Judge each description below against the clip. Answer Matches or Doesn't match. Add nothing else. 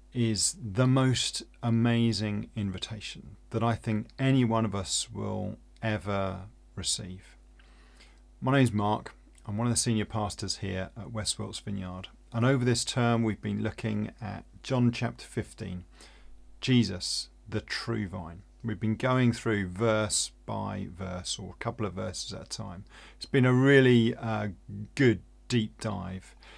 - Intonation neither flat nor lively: Matches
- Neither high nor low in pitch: Doesn't match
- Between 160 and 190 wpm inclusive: Doesn't match